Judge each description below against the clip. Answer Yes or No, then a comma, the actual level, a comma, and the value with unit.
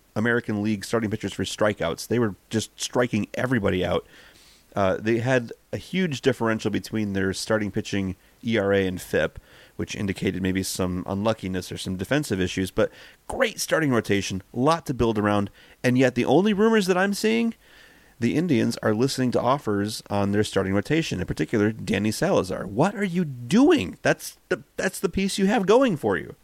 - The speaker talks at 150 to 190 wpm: Yes, average, 180 wpm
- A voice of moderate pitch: No, low, 110 Hz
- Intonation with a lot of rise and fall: Yes, wide, 5.8 semitones